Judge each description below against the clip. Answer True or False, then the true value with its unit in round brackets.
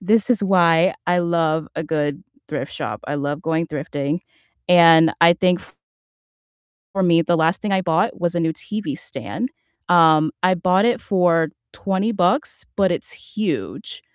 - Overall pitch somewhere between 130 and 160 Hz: False (175 Hz)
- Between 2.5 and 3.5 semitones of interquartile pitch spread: True (2.8 semitones)